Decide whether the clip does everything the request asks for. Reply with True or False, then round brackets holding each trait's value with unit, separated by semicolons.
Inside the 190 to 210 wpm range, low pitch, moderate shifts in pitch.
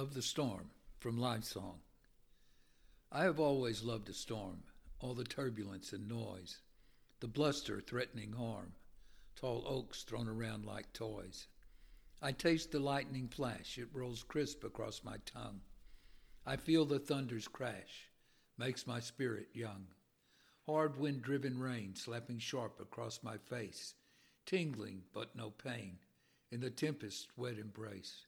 False (135 wpm; 120 Hz; 4.1 semitones)